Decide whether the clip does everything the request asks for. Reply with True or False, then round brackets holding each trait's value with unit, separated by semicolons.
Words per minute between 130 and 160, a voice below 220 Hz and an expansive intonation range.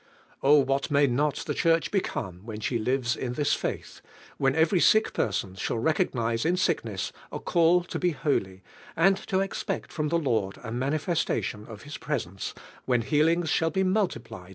False (180 wpm; 140 Hz; 6.4 semitones)